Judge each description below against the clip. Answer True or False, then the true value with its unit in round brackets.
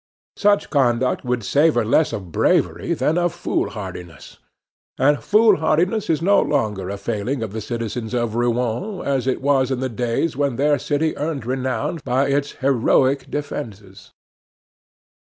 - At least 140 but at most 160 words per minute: True (150 wpm)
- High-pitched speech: False (130 Hz)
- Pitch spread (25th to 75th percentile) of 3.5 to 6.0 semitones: True (4.2 semitones)